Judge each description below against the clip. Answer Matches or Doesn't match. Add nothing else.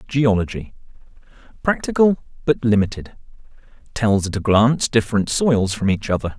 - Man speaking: Matches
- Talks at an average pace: Doesn't match